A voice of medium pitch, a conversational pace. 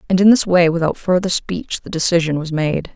No: medium, 175 Hz; fast, 225 wpm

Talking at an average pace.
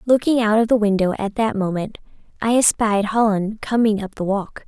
Yes: average, 190 wpm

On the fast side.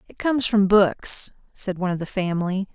No: average, 195 wpm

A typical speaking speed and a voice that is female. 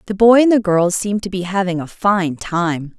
No: fast, 240 wpm; female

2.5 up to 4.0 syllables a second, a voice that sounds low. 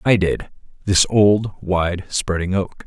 Yes: 3.5 syllables/s; very low, 95 Hz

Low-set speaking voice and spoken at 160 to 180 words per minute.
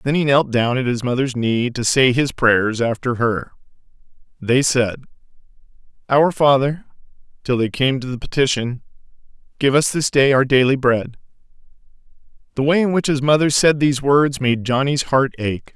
Yes: low, 130 Hz; average, 170 wpm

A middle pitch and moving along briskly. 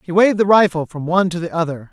Yes: medium, 175 Hz; fast, 280 wpm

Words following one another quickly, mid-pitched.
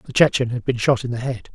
No: fast, 310 wpm; low, 120 Hz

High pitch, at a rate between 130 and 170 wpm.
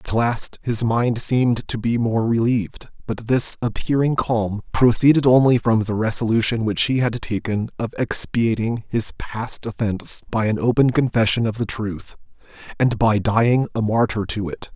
No: low, 115 Hz; average, 165 wpm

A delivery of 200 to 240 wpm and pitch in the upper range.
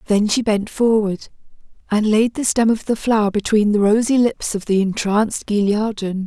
No: average, 180 wpm; high, 215 Hz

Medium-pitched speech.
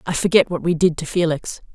Yes: medium, 165 Hz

